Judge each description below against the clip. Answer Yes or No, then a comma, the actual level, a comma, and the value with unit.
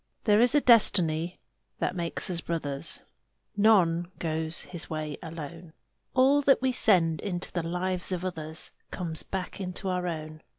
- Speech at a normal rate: Yes, average, 155 wpm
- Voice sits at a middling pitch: Yes, medium, 175 Hz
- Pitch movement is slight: No, average, 3.1 semitones